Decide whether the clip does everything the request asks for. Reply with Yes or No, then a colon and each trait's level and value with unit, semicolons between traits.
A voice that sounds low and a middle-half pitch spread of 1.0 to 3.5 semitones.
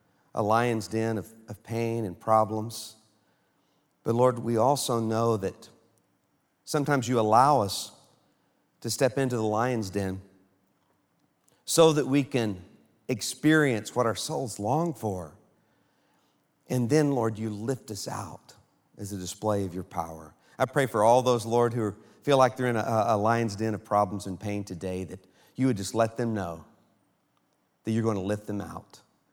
Yes: low, 110 Hz; average, 3.2 semitones